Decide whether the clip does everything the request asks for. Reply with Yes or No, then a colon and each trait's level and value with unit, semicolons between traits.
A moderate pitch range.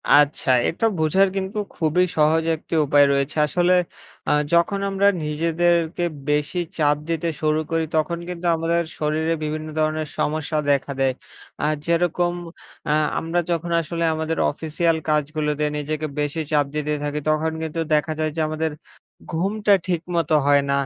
No: narrow, 2.0 semitones